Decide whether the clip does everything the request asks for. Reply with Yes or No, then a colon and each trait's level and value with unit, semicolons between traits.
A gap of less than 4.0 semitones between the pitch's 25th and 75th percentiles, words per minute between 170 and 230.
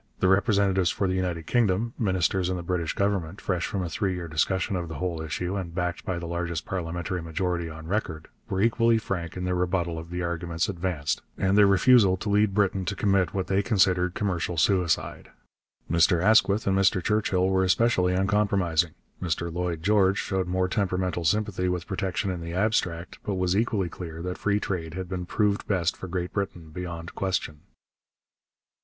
Yes: narrow, 2.4 semitones; average, 185 wpm